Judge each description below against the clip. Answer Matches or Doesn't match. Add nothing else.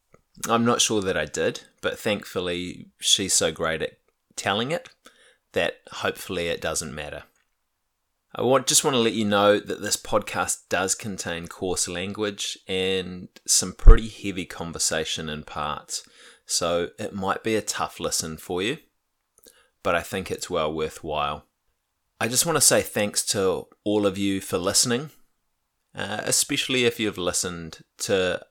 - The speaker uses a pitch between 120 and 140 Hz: Doesn't match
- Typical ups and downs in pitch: Matches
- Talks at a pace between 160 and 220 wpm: Doesn't match